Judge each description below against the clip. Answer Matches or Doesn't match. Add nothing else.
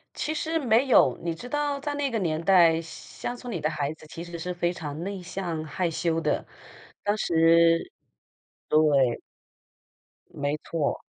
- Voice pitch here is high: Doesn't match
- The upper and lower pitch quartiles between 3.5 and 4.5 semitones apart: Doesn't match